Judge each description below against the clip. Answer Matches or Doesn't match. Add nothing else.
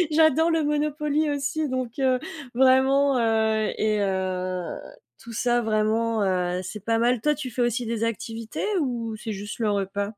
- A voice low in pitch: Doesn't match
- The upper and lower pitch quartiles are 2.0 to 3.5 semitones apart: Doesn't match